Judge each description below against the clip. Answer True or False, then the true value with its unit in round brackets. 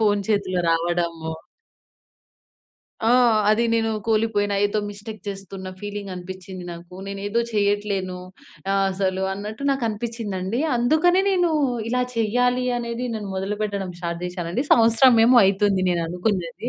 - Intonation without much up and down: False (3.3 semitones)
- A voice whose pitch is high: True (205 Hz)